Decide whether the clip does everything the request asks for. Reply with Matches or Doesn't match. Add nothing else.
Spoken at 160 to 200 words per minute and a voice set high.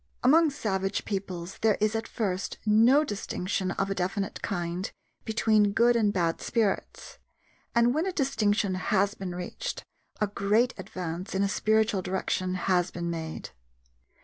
Doesn't match